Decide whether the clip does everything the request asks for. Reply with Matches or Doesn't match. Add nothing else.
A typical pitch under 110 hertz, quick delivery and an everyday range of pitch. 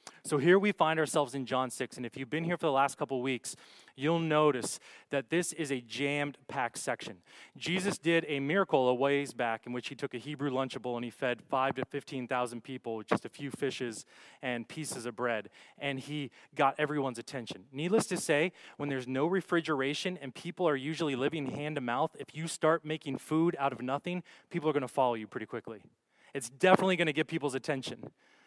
Doesn't match